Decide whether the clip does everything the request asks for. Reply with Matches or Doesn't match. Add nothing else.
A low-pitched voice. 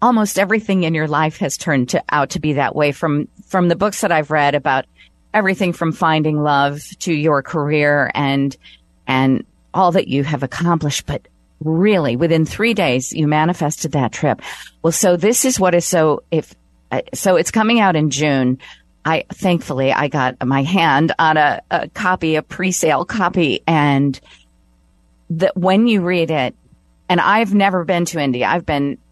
Doesn't match